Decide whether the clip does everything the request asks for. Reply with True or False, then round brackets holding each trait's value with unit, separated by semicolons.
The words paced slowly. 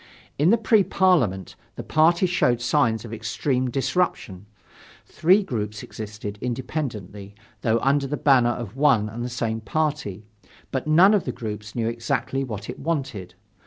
False (155 wpm)